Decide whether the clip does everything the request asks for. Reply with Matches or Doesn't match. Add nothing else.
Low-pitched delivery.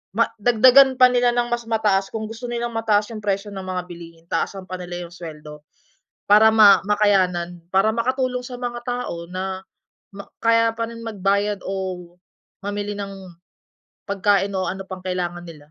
Doesn't match